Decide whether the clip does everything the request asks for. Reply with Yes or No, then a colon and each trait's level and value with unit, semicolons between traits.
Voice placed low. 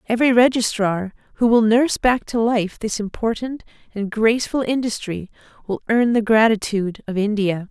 No: high, 220 Hz